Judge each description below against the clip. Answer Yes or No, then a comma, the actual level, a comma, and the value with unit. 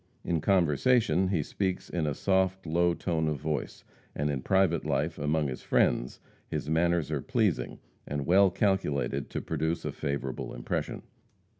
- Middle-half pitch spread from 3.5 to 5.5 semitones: Yes, average, 4.3 semitones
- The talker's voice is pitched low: Yes, very low, 80 Hz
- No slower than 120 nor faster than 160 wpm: Yes, average, 155 wpm